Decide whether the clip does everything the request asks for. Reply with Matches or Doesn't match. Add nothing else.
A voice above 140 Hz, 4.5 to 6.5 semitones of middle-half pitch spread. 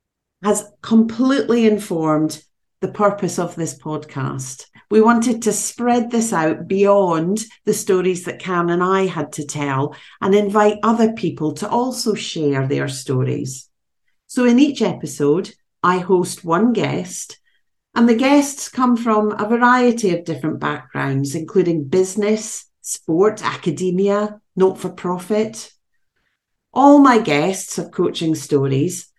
Matches